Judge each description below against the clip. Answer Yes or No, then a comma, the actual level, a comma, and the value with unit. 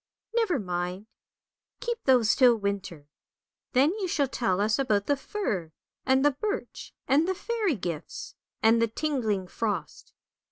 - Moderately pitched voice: No, high, 240 Hz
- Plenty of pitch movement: Yes, wide, 7.2 semitones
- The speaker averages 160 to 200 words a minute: No, average, 150 wpm